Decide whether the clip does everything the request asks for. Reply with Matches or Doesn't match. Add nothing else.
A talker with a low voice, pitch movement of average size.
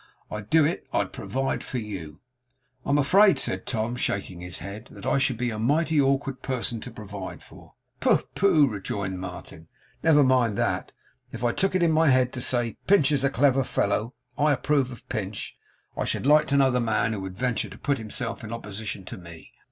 Matches